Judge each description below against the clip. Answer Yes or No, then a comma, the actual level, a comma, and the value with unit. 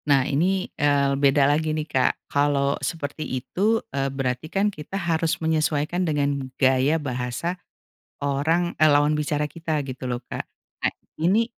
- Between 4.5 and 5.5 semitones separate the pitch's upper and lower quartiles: No, average, 2.8 semitones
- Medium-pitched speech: Yes, medium, 150 Hz